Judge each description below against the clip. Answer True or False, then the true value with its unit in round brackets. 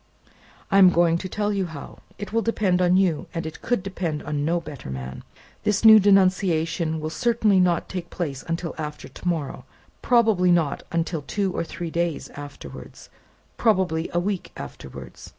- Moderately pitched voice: True (175 Hz)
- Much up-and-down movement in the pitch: False (3.5 semitones)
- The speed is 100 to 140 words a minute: False (175 wpm)